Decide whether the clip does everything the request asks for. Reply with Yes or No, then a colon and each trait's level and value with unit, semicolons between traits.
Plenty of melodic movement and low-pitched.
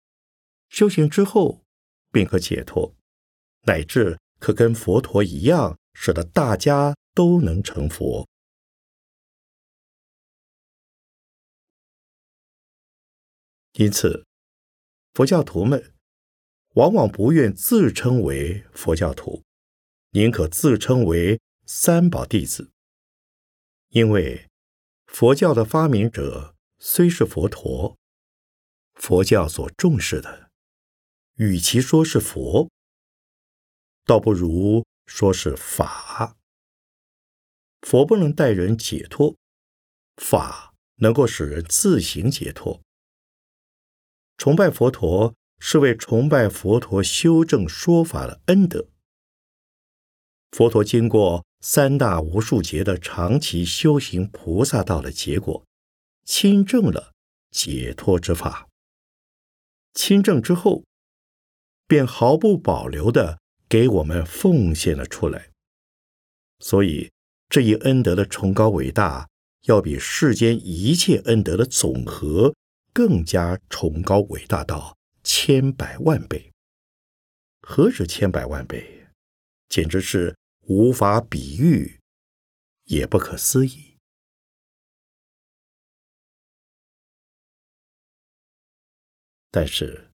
Yes: wide, 7.9 semitones; low, 100 Hz